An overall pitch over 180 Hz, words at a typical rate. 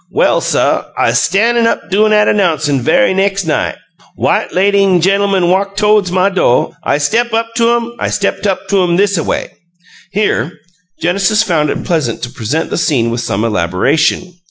Yes: high, 190 Hz; average, 175 wpm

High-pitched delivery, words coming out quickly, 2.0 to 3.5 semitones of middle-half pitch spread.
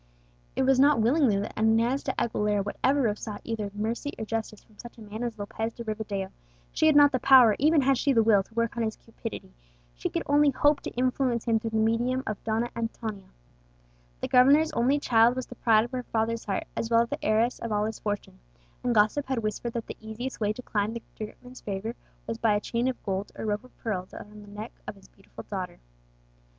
Yes: high, 225 Hz; fast, 235 wpm; average, 2.9 semitones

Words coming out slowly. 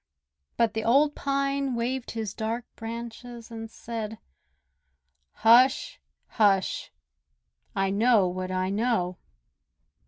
Yes: slow, 100 wpm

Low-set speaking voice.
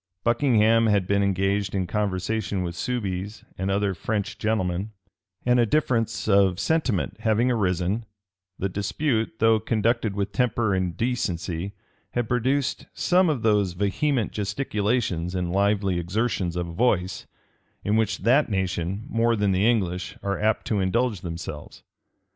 Yes: low, 105 Hz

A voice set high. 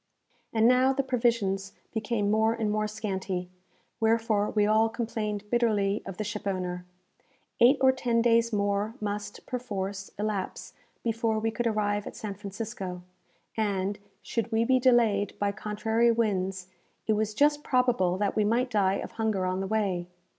Yes: high, 215 Hz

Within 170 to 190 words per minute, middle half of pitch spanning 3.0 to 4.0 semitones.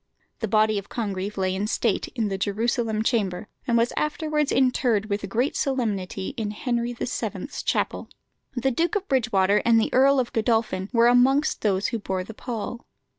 Yes: average, 175 wpm; average, 3.4 semitones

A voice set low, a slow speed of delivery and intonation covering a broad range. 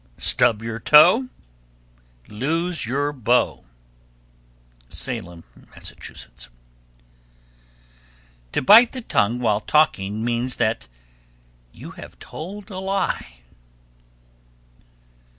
Yes: low, 125 Hz; slow, 85 wpm; wide, 8.0 semitones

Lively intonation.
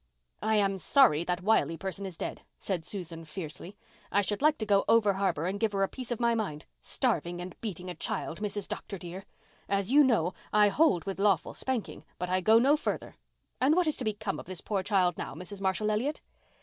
No: average, 3.6 semitones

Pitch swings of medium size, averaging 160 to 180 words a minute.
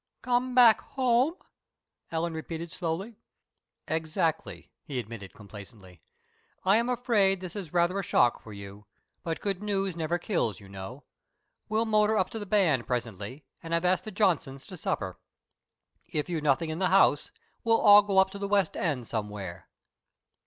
No: wide, 8.1 semitones; average, 165 wpm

